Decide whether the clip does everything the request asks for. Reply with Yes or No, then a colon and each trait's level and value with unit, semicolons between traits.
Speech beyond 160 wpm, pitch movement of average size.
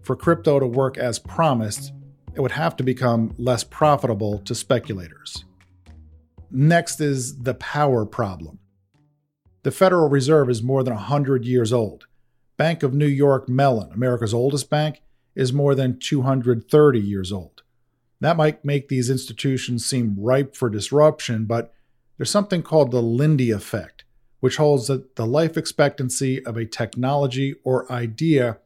No: average, 145 wpm; average, 3.6 semitones